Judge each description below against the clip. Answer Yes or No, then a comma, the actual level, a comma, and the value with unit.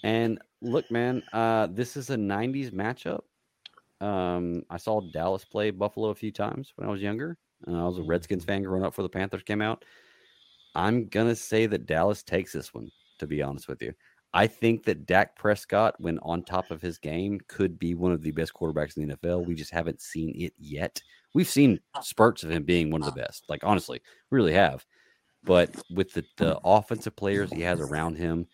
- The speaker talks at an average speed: No, fast, 210 wpm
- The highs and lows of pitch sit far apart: No, average, 4.4 semitones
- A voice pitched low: Yes, very low, 95 Hz